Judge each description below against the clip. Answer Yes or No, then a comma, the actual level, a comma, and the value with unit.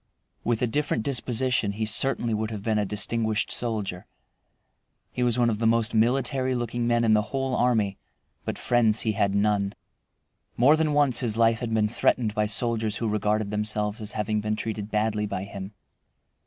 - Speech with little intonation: Yes, narrow, 2.2 semitones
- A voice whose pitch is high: No, low, 110 Hz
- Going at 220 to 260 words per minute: No, average, 180 wpm